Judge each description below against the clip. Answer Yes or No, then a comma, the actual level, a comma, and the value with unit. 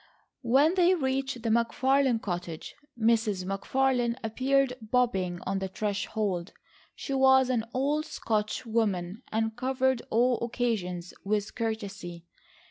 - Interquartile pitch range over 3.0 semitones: Yes, average, 4.7 semitones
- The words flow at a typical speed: No, slow, 120 wpm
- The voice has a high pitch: Yes, high, 230 Hz